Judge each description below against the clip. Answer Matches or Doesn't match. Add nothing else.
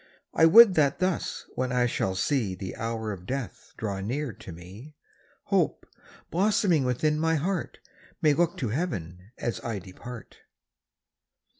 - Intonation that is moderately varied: Doesn't match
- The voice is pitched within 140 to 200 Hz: Doesn't match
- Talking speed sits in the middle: Matches